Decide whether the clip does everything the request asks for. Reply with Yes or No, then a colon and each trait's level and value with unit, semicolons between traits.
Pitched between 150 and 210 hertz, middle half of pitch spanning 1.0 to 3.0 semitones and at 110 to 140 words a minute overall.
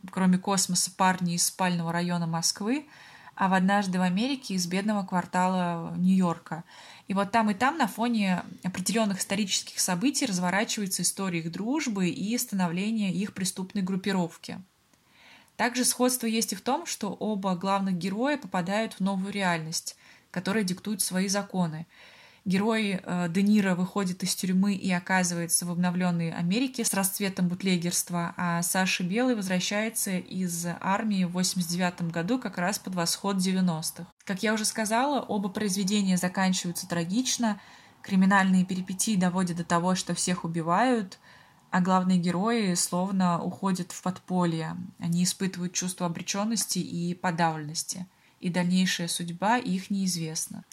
Yes: medium, 185 Hz; narrow, 2.6 semitones; average, 135 wpm